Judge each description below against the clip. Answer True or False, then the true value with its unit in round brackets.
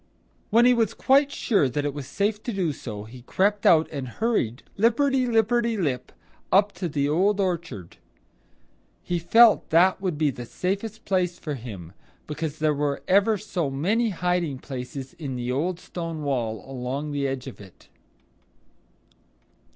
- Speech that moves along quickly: False (165 wpm)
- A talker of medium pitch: True (165 Hz)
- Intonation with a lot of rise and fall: True (7.1 semitones)